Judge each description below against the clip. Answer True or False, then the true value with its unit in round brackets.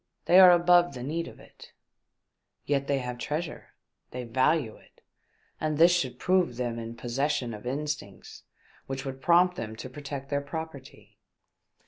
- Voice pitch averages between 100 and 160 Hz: True (140 Hz)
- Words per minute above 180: False (155 wpm)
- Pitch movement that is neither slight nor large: True (4.6 semitones)